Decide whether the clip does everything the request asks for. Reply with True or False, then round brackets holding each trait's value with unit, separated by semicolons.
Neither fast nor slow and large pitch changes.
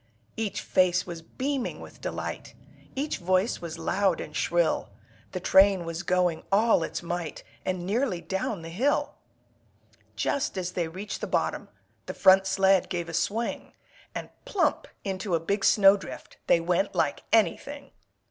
False (150 wpm; 3.1 semitones)